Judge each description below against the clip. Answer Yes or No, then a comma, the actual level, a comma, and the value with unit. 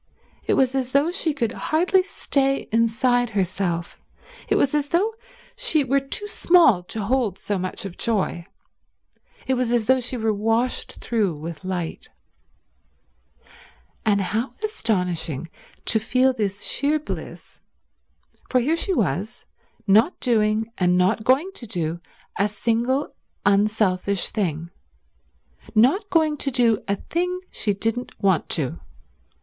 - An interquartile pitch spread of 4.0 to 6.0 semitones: Yes, wide, 5.5 semitones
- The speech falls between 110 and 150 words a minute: Yes, average, 140 wpm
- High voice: Yes, high, 225 Hz